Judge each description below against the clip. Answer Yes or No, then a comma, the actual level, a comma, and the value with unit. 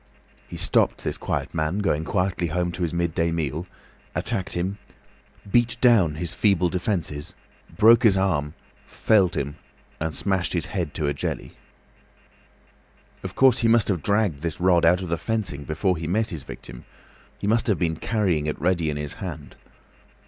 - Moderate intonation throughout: Yes, average, 4.2 semitones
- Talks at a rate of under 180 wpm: Yes, average, 170 wpm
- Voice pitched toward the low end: Yes, very low, 90 Hz